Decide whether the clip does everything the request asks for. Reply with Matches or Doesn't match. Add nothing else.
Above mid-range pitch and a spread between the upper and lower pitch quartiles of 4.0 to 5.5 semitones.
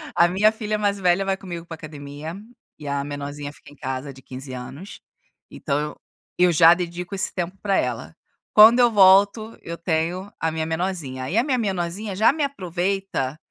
Doesn't match